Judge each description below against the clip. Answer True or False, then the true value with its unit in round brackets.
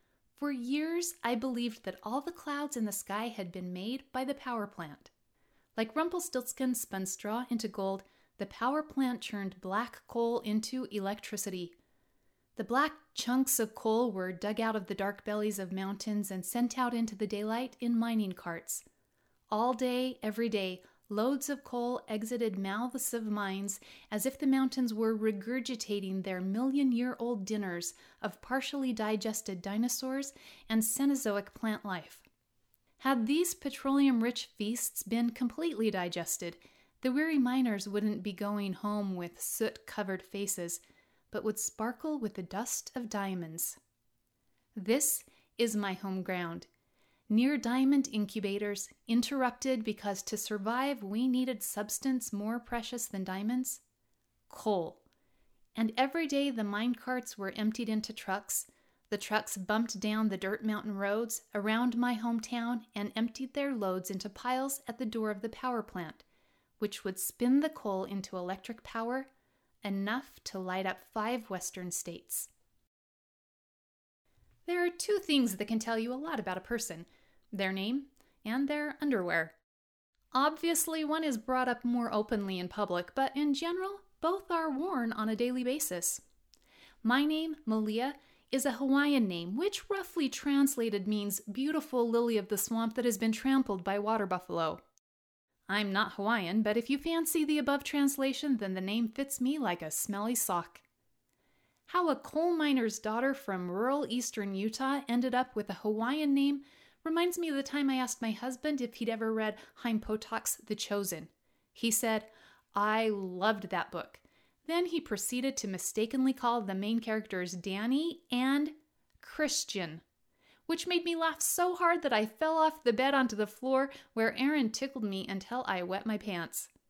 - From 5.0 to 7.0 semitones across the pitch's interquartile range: False (4.5 semitones)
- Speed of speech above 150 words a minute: True (160 wpm)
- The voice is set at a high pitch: True (230 Hz)